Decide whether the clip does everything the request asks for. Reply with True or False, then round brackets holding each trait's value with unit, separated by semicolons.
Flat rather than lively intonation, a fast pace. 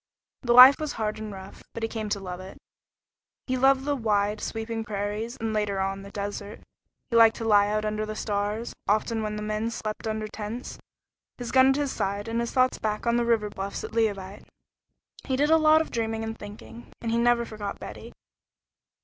True (2.3 semitones; 210 wpm)